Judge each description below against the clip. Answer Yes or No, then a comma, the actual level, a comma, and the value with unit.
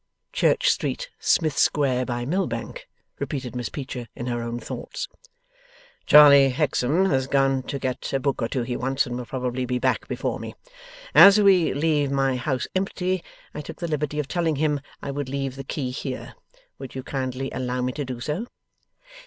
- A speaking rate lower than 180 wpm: No, average, 185 wpm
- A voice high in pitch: No, low, 135 Hz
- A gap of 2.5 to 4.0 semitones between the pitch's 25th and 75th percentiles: Yes, average, 2.9 semitones